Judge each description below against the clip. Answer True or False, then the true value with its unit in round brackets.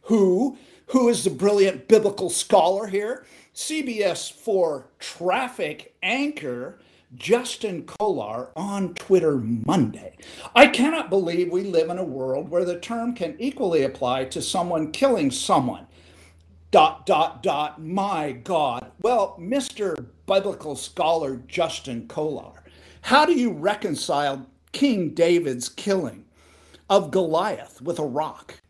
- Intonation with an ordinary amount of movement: False (6.3 semitones)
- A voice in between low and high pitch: True (180 Hz)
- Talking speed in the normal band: False (120 wpm)